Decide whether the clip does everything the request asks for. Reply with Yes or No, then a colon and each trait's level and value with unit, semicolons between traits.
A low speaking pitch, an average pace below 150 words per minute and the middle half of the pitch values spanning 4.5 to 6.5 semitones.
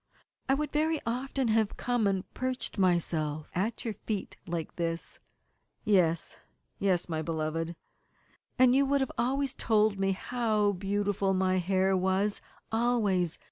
No: high, 200 Hz; average, 140 wpm; average, 4.9 semitones